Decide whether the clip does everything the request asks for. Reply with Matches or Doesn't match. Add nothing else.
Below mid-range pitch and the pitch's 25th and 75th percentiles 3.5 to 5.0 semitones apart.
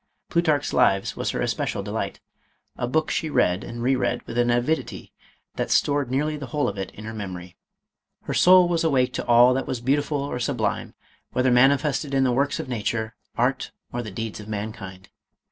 Matches